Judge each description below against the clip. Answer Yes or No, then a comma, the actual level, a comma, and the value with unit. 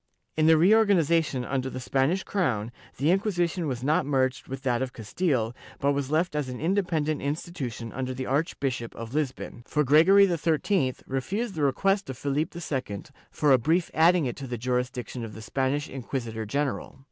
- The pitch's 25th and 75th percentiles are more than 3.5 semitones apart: Yes, average, 4.5 semitones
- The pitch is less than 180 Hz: Yes, medium, 140 Hz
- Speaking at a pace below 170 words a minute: No, average, 175 wpm